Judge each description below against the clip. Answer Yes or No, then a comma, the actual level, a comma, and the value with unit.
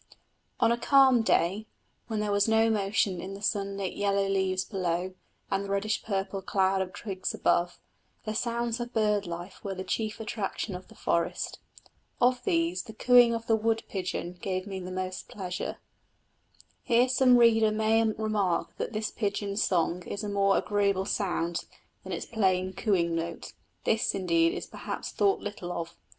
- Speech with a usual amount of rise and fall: Yes, average, 3.0 semitones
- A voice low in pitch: No, high, 200 Hz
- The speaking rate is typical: Yes, average, 170 wpm